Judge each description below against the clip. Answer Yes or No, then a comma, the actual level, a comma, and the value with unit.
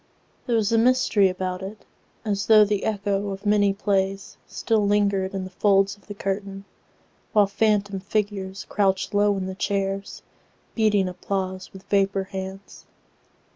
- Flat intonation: Yes, narrow, 1.2 semitones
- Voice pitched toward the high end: Yes, high, 200 Hz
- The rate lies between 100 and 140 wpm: Yes, slow, 135 wpm